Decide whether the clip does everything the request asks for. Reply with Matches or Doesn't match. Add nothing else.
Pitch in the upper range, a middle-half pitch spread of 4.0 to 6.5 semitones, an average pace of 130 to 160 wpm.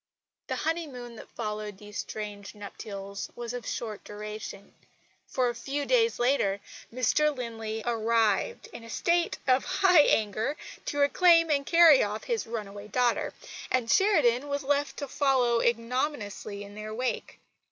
Matches